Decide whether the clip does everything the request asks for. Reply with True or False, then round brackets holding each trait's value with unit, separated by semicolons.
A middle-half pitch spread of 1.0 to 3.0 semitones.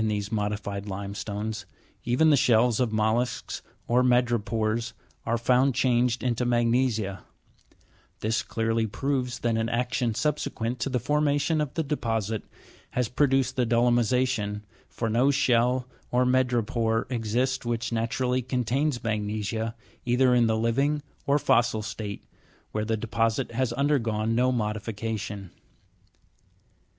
True (2.4 semitones)